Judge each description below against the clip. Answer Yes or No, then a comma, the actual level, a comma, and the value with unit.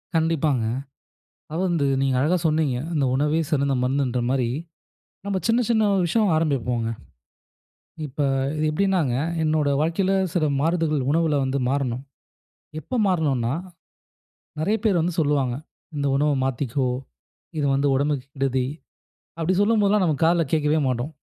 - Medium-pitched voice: Yes, medium, 150 Hz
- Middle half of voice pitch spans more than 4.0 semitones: No, average, 3.7 semitones